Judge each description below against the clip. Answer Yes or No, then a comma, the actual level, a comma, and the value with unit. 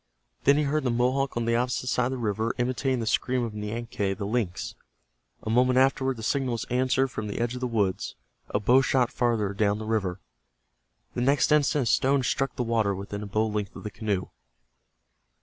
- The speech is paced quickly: Yes, fast, 210 wpm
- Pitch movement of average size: Yes, average, 3.4 semitones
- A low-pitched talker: Yes, low, 120 Hz